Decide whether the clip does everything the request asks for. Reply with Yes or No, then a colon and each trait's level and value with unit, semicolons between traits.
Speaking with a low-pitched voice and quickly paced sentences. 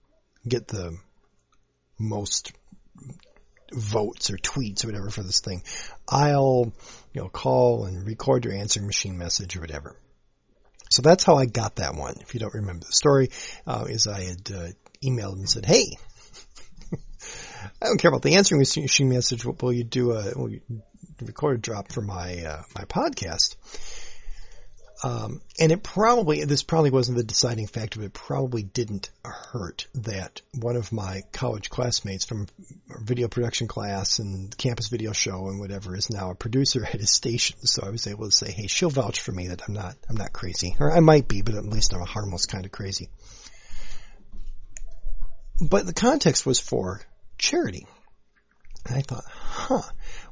No: low, 110 Hz; average, 170 wpm